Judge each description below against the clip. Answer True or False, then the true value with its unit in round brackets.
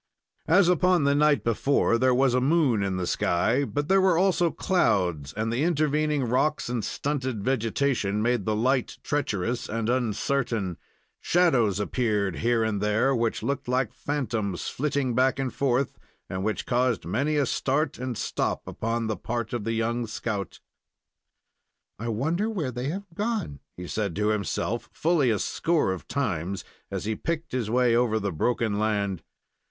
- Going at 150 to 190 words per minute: True (165 wpm)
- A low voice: True (120 Hz)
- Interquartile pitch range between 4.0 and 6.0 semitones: True (4.8 semitones)